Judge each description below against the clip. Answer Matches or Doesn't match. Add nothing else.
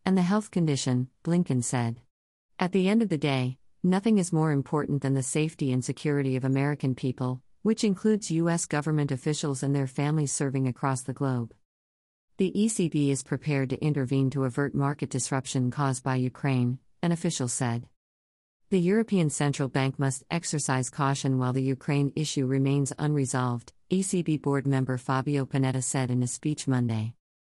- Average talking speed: Matches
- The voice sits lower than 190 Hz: Matches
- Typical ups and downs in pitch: Matches